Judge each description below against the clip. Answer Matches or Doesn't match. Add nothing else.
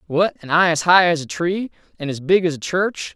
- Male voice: Matches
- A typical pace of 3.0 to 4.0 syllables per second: Doesn't match